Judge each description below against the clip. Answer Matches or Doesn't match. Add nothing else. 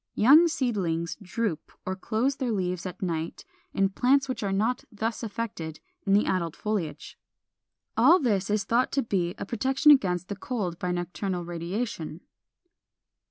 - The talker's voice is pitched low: Doesn't match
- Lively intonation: Doesn't match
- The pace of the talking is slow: Doesn't match